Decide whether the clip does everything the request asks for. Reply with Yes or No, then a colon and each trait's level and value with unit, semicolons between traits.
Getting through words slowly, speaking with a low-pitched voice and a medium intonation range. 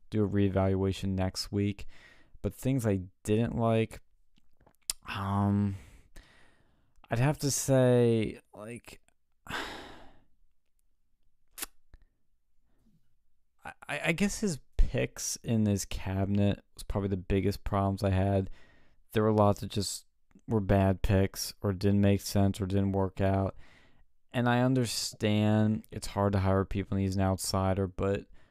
No: slow, 125 wpm; low, 100 Hz; narrow, 2.0 semitones